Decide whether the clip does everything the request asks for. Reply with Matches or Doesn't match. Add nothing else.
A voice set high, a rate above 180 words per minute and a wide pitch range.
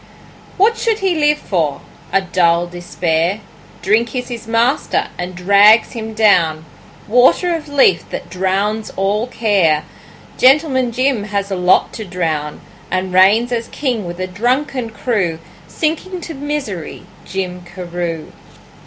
Doesn't match